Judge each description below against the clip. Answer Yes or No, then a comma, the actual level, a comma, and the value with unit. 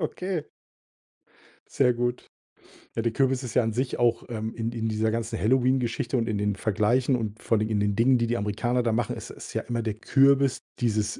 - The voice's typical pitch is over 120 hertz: No, low, 115 Hz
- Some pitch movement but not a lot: No, narrow, 2.3 semitones